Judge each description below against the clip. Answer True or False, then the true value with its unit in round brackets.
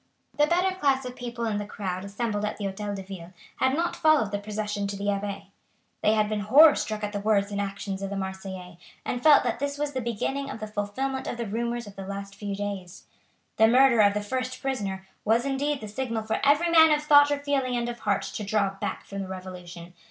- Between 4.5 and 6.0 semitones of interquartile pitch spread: True (4.8 semitones)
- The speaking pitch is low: False (215 Hz)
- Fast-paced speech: True (235 wpm)